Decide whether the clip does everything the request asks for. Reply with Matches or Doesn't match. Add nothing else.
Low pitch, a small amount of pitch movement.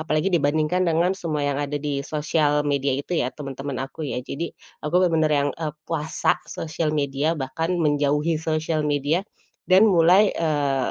Doesn't match